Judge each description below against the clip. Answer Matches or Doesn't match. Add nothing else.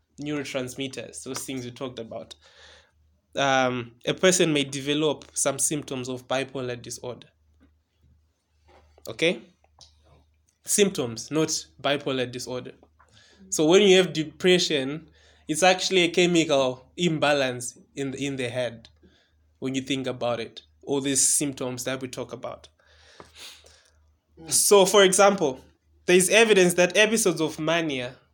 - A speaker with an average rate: Doesn't match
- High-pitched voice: Doesn't match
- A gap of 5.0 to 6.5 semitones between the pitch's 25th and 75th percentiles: Matches